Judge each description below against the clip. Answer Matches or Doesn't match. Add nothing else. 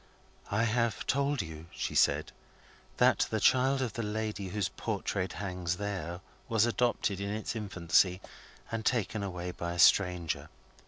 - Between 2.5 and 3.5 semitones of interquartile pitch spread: Doesn't match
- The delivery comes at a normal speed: Matches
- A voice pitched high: Doesn't match